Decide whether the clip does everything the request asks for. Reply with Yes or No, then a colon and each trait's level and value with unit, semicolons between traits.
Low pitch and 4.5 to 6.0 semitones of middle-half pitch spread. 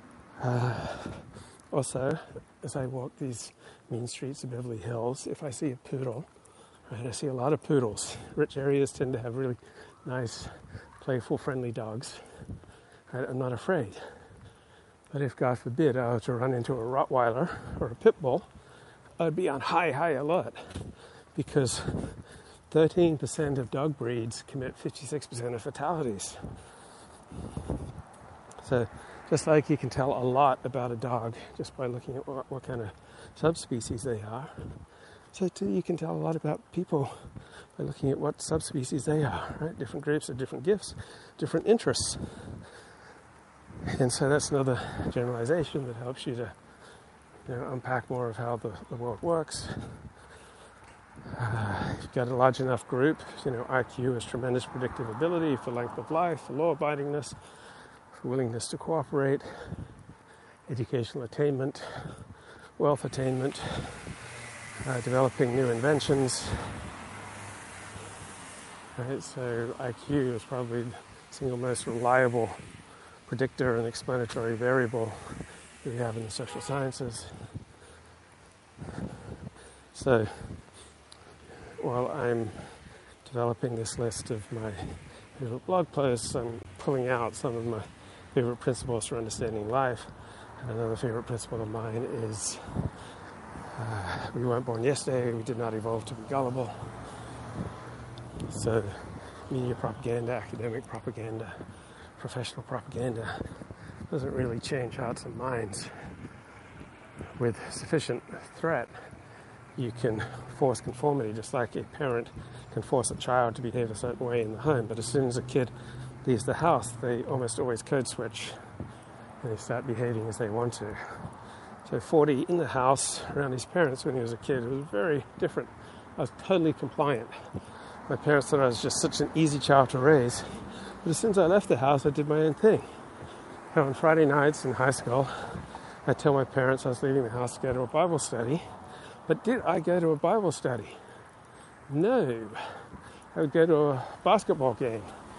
No: low, 125 Hz; average, 3.5 semitones